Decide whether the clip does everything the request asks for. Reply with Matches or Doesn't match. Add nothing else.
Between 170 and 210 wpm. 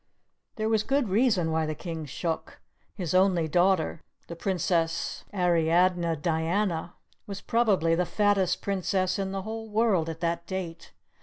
Doesn't match